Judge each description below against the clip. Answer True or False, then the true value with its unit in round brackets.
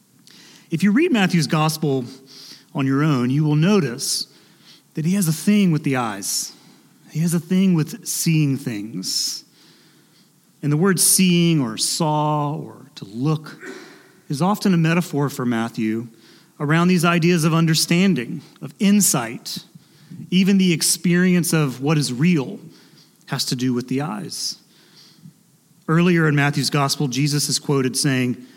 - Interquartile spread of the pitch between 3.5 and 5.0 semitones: True (4.0 semitones)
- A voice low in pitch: False (160 Hz)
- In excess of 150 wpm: False (145 wpm)